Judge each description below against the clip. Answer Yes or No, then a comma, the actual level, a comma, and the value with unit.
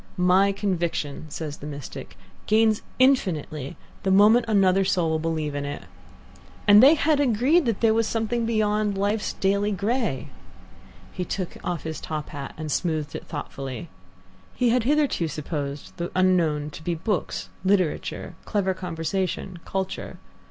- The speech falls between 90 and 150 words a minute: Yes, average, 145 wpm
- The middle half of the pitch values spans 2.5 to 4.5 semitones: No, average, 5.3 semitones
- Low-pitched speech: No, medium, 185 Hz